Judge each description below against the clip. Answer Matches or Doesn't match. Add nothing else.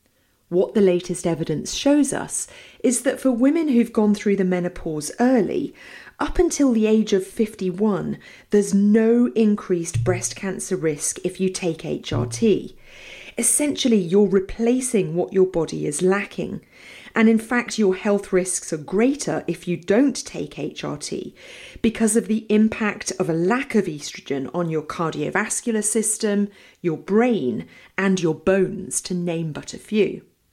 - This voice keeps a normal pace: Matches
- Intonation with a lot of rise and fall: Doesn't match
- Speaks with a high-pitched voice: Matches